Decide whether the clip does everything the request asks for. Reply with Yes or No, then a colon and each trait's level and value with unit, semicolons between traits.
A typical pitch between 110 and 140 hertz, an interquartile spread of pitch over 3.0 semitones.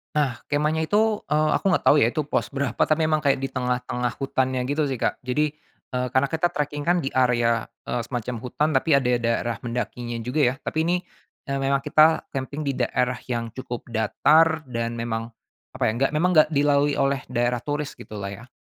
Yes: low, 135 Hz; average, 3.7 semitones